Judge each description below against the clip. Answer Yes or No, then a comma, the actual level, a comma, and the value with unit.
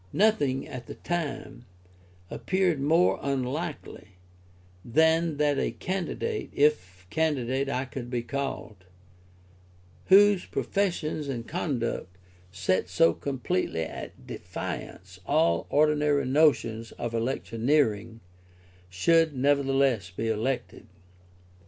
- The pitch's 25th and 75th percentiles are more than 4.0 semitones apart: Yes, average, 5.1 semitones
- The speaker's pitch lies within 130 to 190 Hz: Yes, low, 135 Hz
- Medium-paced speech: No, slow, 95 wpm